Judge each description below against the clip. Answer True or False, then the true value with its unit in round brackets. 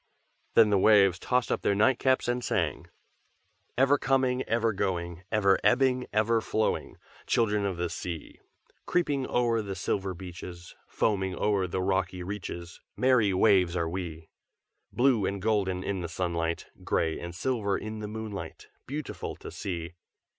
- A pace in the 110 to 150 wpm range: True (145 wpm)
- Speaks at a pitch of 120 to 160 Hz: False (100 Hz)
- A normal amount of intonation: True (4.2 semitones)